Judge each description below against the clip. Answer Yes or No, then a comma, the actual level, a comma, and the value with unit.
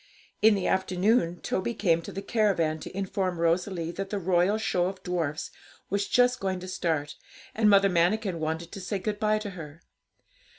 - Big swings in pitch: No, average, 3.3 semitones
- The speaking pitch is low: No, medium, 185 Hz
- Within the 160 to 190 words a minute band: Yes, average, 180 wpm